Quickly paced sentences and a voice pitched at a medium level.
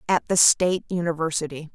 No: slow, 135 wpm; medium, 165 Hz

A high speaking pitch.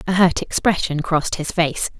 No: medium, 170 Hz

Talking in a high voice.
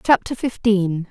Yes: high, 210 Hz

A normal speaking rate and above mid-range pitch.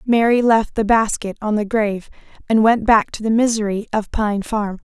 Yes: average, 195 wpm; high, 215 Hz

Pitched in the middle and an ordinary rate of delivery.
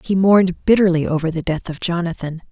Yes: medium, 175 Hz; average, 190 wpm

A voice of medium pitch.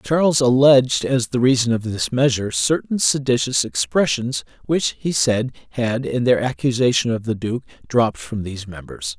No: low, 125 Hz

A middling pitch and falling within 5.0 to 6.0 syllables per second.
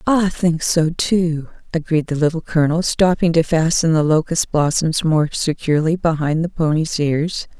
No: medium, 160 Hz; 4.7 syllables/s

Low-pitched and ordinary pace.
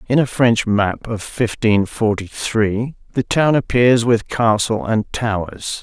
Yes: low, 115 Hz; average, 155 wpm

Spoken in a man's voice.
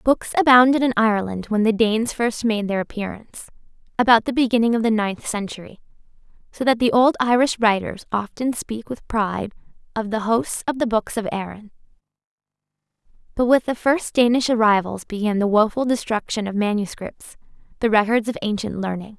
No: female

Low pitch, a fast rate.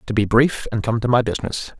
Yes: low, 115 Hz; fast, 265 wpm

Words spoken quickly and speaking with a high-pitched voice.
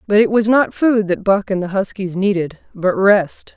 Yes: fast, 220 wpm; high, 195 Hz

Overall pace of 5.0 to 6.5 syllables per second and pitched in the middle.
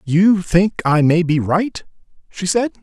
No: 3.8 syllables/s; medium, 180 Hz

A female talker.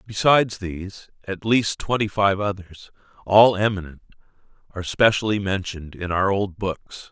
No: male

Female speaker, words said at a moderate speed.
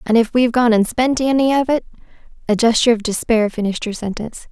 No: female; fast, 215 wpm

